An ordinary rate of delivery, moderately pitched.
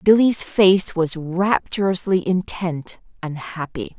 No: slow, 105 wpm; medium, 180 Hz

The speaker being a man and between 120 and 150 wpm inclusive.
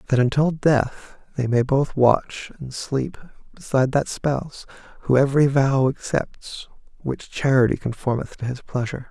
Yes: male; average, 145 wpm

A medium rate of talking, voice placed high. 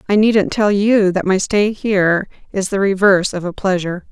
No: fast, 220 wpm; high, 195 Hz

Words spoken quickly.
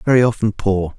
No: average, 185 wpm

